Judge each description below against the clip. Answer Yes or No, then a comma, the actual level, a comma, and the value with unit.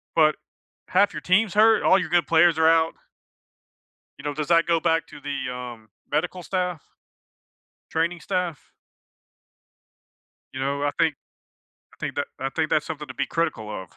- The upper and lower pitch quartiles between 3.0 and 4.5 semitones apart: Yes, average, 3.6 semitones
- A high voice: No, medium, 160 Hz